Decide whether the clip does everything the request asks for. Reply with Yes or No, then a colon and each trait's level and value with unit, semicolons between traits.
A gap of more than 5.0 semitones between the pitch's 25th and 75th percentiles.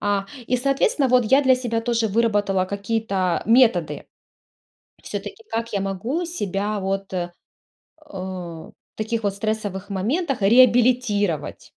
No: average, 4.0 semitones